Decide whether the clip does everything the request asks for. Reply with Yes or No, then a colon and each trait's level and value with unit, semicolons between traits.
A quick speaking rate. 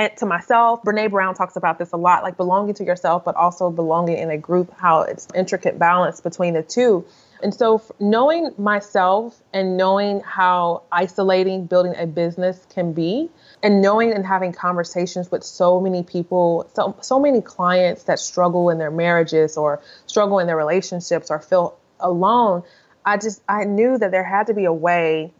No: average, 180 wpm